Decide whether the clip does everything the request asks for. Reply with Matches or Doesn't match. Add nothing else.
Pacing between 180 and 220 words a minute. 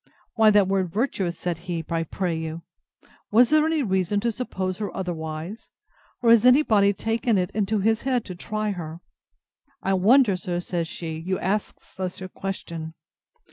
Doesn't match